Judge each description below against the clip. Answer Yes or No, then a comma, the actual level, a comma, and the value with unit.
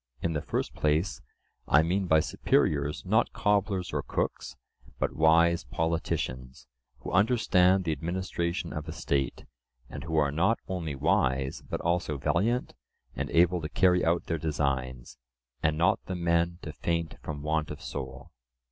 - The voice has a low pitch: Yes, very low, 80 Hz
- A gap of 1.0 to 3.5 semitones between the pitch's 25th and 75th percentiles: Yes, average, 3.2 semitones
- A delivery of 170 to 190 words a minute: No, average, 155 wpm